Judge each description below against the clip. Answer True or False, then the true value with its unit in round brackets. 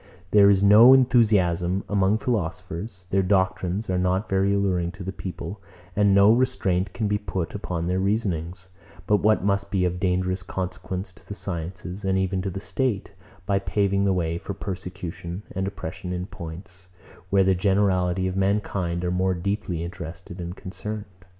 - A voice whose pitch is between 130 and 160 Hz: False (95 Hz)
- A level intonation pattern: True (1.9 semitones)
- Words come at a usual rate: True (170 wpm)